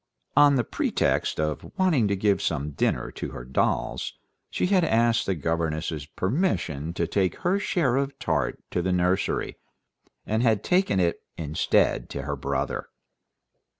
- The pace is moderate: Yes, average, 150 wpm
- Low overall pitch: Yes, very low, 95 Hz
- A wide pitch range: Yes, wide, 8.7 semitones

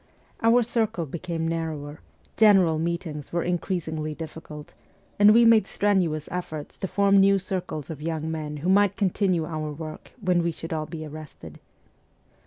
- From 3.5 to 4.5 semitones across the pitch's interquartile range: Yes, average, 3.8 semitones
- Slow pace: No, average, 155 wpm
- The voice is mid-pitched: Yes, medium, 165 Hz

